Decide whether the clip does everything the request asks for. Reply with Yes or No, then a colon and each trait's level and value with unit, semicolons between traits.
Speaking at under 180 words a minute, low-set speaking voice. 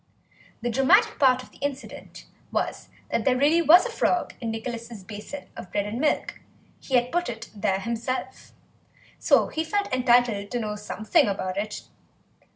No: average, 165 wpm; high, 245 Hz